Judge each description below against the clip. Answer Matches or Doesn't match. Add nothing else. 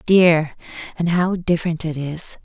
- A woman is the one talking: Matches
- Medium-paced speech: Matches